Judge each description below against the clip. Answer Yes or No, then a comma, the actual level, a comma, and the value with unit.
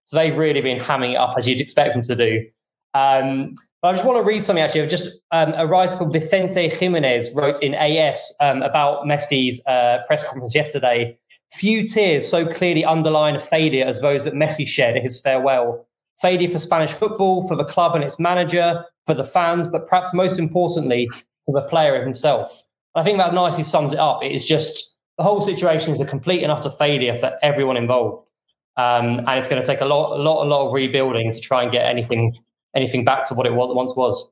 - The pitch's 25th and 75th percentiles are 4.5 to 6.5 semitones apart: Yes, average, 4.8 semitones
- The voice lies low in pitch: No, medium, 150 Hz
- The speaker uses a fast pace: Yes, fast, 215 wpm